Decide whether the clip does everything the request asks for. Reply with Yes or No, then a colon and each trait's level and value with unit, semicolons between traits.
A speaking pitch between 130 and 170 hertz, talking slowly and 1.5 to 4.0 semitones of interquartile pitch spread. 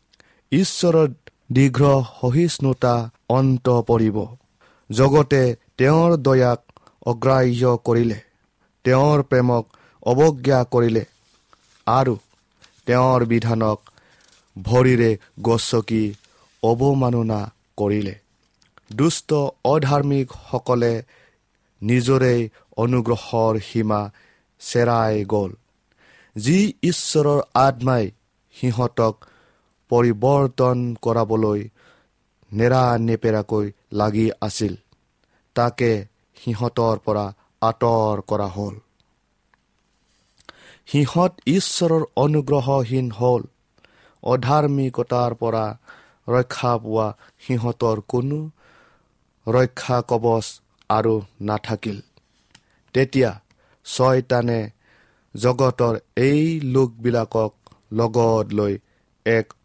No: low, 120 Hz; slow, 65 wpm; average, 2.9 semitones